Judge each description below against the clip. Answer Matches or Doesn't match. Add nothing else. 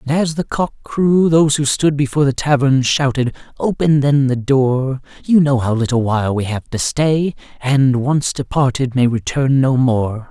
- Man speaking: Matches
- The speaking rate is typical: Matches